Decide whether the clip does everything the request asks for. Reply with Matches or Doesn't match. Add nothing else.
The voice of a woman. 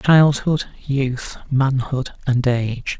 Doesn't match